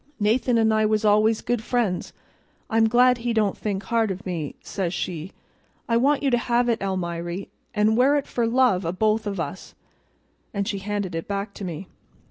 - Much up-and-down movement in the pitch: No, average, 3.4 semitones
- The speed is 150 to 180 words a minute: No, average, 195 wpm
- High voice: Yes, high, 215 Hz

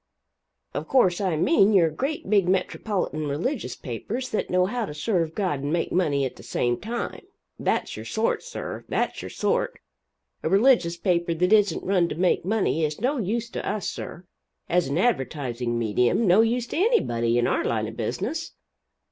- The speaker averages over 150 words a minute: Yes, average, 180 wpm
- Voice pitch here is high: No, medium, 180 Hz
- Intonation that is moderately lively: No, wide, 7.2 semitones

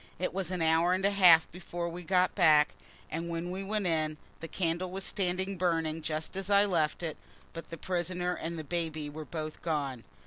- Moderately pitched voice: Yes, medium, 170 Hz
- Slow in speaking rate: No, fast, 205 wpm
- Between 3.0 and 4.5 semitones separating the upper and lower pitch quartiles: No, narrow, 2.5 semitones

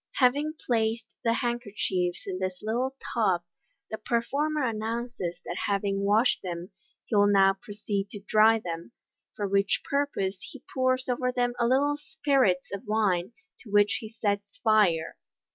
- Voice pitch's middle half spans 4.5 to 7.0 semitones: No, average, 3.8 semitones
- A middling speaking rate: Yes, average, 150 wpm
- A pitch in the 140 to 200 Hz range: No, high, 215 Hz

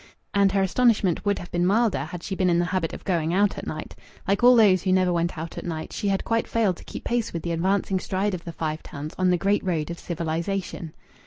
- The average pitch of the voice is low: No, medium, 185 Hz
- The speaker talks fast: Yes, fast, 260 wpm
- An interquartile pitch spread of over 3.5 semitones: No, average, 2.9 semitones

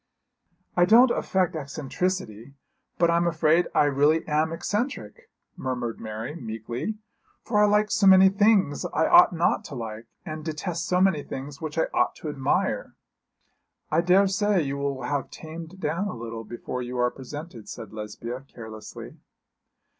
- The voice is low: No, medium, 155 Hz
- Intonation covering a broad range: Yes, wide, 6.7 semitones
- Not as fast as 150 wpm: No, average, 155 wpm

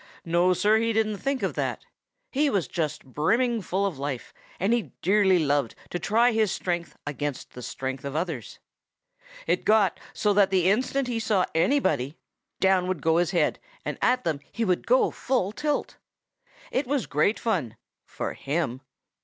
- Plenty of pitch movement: Yes, wide, 6.3 semitones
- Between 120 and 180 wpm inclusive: Yes, average, 170 wpm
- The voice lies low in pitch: No, medium, 185 Hz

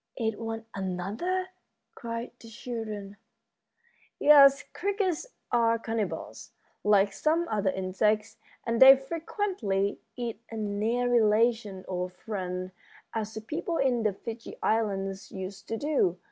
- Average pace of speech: No, slow, 125 wpm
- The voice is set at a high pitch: Yes, high, 225 Hz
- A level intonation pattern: No, average, 3.7 semitones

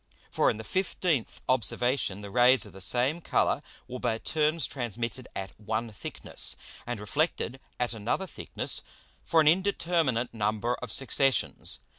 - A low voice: Yes, low, 125 Hz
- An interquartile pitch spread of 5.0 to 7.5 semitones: Yes, average, 5.3 semitones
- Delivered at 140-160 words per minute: Yes, average, 145 wpm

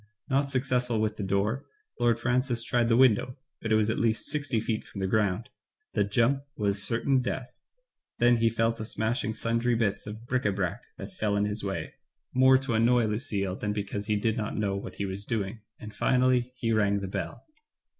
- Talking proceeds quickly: Yes, fast, 215 wpm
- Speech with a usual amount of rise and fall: Yes, average, 3.1 semitones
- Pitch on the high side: No, low, 115 Hz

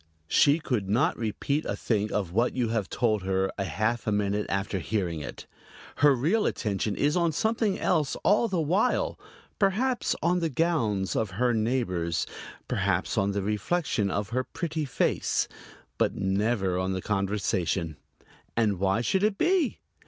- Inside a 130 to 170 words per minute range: Yes, average, 160 wpm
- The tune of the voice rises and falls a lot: Yes, wide, 8.2 semitones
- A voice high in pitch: No, low, 110 Hz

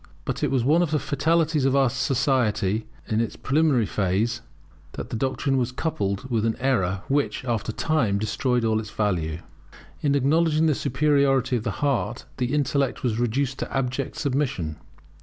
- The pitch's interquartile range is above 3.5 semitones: Yes, average, 4.4 semitones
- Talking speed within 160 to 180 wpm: Yes, average, 170 wpm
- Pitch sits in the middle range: No, low, 130 Hz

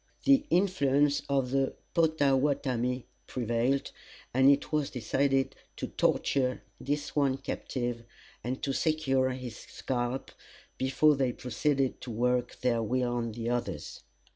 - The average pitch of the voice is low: Yes, low, 130 Hz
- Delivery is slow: Yes, slow, 125 wpm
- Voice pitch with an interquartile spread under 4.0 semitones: Yes, narrow, 2.4 semitones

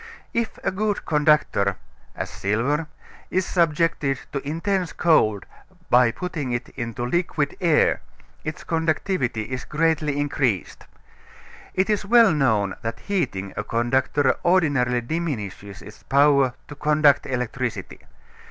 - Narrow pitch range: No, wide, 5.5 semitones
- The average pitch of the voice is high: No, medium, 145 Hz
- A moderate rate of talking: No, slow, 120 wpm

